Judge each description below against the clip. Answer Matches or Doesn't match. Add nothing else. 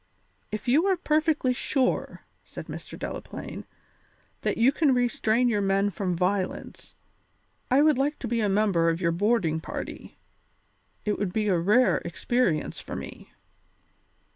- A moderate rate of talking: Matches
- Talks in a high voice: Matches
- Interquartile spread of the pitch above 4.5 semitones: Matches